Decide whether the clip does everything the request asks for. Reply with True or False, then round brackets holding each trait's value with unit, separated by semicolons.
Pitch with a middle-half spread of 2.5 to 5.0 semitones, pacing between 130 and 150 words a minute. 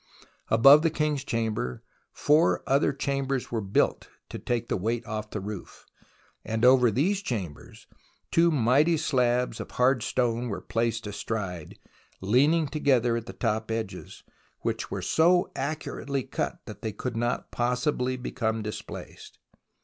True (3.9 semitones; 140 wpm)